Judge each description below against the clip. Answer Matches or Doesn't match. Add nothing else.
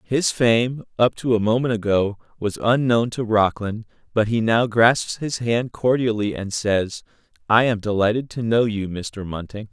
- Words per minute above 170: Doesn't match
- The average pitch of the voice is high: Doesn't match